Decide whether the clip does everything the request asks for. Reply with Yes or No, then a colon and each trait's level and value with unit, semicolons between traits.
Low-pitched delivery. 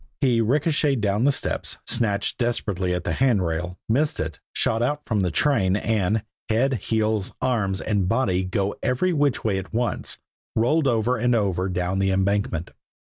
Yes: low, 110 Hz